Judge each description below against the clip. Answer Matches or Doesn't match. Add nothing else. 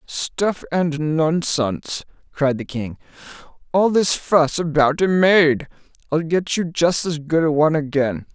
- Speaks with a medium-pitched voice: Matches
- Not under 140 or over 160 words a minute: Matches